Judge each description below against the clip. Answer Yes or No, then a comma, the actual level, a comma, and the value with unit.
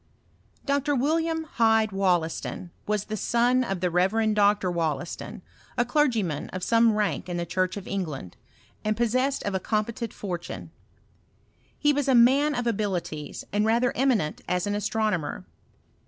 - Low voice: No, high, 210 Hz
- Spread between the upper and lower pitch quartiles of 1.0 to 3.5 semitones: No, average, 4.8 semitones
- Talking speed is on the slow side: No, average, 155 wpm